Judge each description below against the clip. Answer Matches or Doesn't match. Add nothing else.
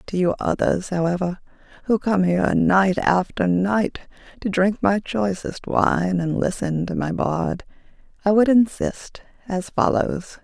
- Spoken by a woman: Matches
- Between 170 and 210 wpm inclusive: Doesn't match